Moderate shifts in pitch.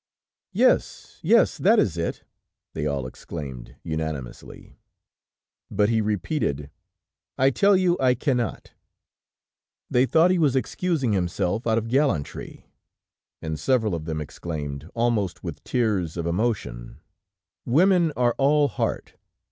No: wide, 9.0 semitones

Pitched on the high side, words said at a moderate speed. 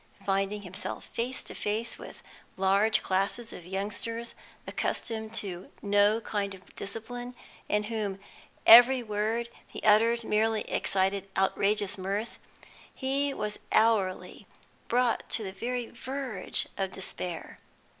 No: high, 210 Hz; slow, 120 wpm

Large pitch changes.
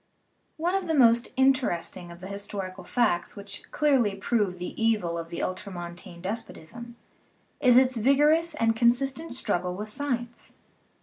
Yes: wide, 6.0 semitones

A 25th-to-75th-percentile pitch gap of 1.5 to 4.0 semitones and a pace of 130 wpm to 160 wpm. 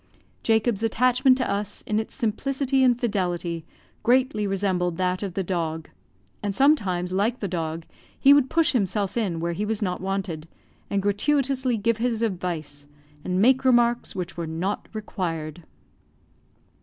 No: average, 5.2 semitones; average, 150 wpm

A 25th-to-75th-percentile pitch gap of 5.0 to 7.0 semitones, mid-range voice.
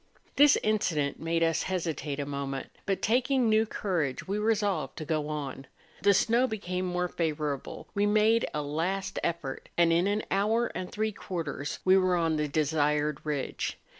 Yes: wide, 5.4 semitones; medium, 175 Hz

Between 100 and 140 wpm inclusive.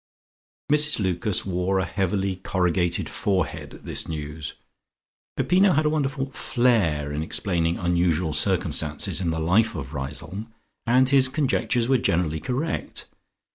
Yes: slow, 135 wpm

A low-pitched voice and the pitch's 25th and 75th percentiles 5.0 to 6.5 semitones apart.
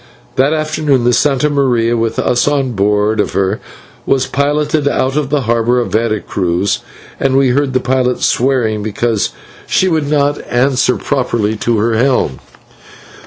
No: low, 125 Hz; average, 3.8 semitones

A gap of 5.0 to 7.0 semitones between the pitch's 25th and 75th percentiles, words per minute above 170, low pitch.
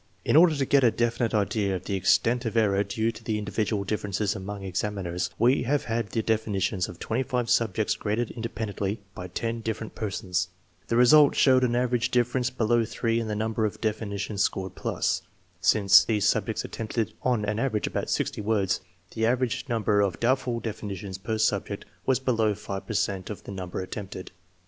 No: average, 2.8 semitones; average, 185 wpm; low, 110 Hz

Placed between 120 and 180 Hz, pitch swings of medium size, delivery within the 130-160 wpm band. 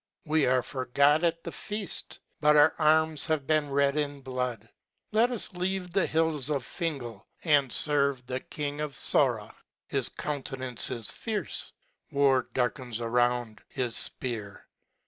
Yes: medium, 140 Hz; average, 3.8 semitones; average, 145 wpm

